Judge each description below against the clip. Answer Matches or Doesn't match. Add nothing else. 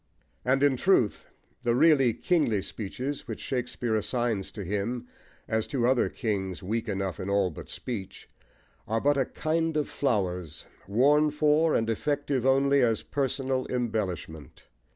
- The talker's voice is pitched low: Matches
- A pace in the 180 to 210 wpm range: Doesn't match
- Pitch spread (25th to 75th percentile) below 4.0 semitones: Doesn't match